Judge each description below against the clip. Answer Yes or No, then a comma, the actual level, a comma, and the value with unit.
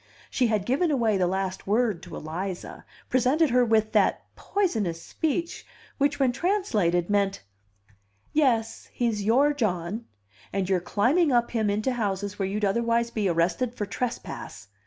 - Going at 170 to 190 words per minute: No, average, 150 wpm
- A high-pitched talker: Yes, high, 220 Hz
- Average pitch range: Yes, average, 4.5 semitones